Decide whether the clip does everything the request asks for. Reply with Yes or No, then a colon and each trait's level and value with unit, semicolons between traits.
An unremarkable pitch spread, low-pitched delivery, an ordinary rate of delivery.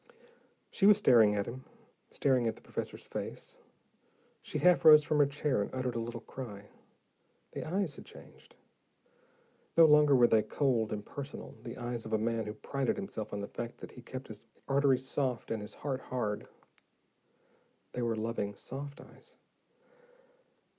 Yes: average, 3.9 semitones; low, 125 Hz; average, 165 wpm